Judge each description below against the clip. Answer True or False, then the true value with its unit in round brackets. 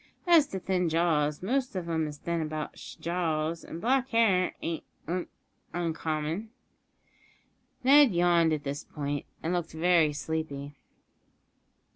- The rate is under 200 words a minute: True (135 wpm)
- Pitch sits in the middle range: True (170 Hz)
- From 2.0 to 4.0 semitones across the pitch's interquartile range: True (2.9 semitones)